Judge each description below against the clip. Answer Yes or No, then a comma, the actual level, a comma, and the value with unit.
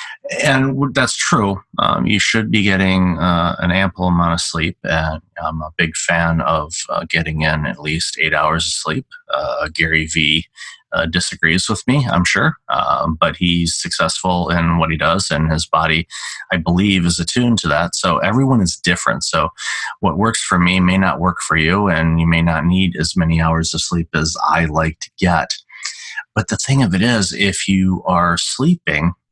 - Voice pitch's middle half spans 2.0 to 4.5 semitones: Yes, average, 2.8 semitones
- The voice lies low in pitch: Yes, very low, 85 Hz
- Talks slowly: No, average, 190 wpm